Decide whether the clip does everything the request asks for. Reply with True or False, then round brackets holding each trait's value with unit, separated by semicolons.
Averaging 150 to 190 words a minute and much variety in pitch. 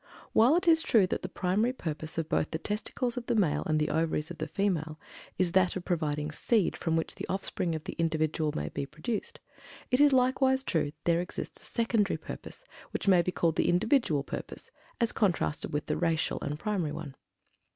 False (205 wpm; 6.0 semitones)